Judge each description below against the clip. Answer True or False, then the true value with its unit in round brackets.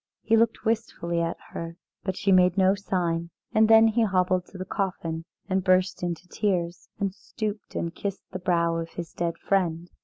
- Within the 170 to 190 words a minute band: True (185 wpm)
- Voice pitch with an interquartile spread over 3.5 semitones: False (2.8 semitones)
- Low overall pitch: False (185 Hz)